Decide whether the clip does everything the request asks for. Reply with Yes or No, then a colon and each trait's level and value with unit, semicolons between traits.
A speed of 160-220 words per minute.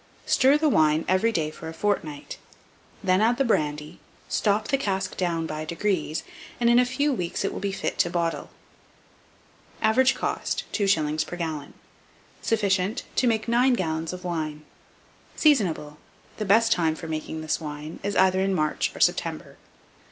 Yes: average, 165 wpm